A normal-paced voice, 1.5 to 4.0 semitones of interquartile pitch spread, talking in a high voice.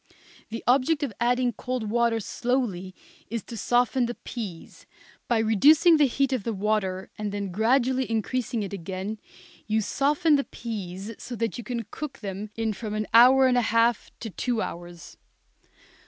Yes: average, 170 wpm; average, 3.4 semitones; high, 230 Hz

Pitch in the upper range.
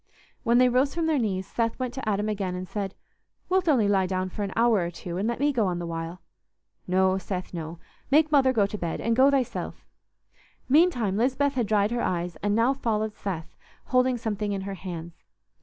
Yes: high, 210 Hz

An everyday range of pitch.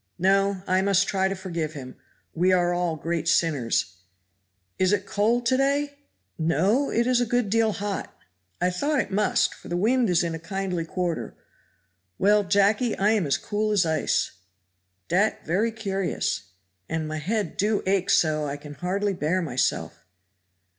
Yes: average, 4.1 semitones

